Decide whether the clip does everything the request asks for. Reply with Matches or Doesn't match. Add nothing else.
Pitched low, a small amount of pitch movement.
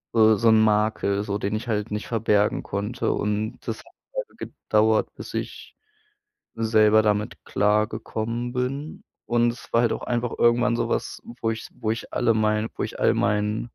Matches